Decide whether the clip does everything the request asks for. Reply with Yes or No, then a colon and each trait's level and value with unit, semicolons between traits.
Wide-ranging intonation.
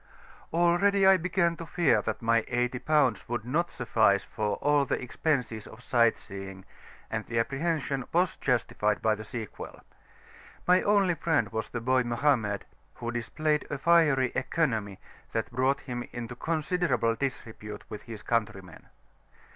Yes: wide, 5.8 semitones